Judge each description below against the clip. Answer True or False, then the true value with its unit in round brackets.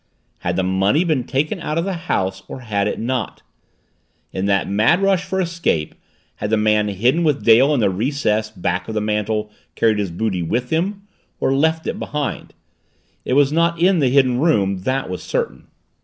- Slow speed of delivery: False (190 wpm)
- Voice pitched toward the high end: False (120 Hz)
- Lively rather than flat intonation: True (7.1 semitones)